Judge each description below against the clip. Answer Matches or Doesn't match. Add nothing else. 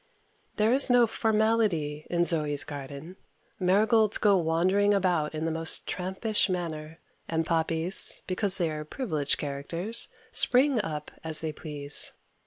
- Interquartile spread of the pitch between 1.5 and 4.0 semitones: Doesn't match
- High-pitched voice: Doesn't match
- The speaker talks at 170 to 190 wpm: Doesn't match